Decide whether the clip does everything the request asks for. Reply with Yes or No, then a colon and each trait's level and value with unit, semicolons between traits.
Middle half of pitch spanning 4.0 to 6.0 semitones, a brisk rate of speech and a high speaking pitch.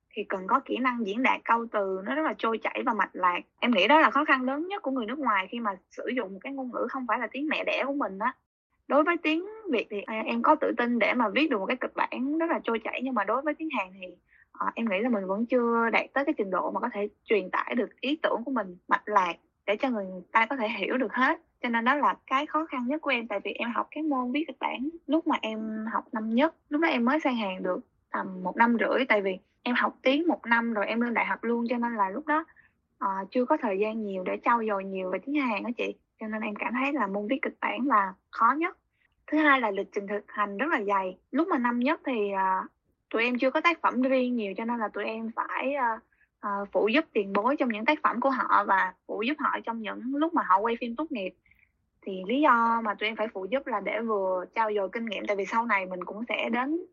Yes: wide, 5.5 semitones; fast, 280 wpm; high, 240 Hz